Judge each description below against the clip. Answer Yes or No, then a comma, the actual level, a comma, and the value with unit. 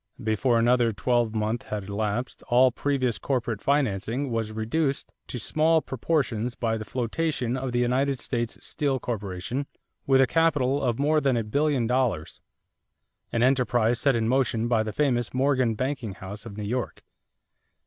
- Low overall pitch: Yes, low, 125 Hz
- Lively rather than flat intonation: No, average, 3.2 semitones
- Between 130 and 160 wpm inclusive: Yes, average, 155 wpm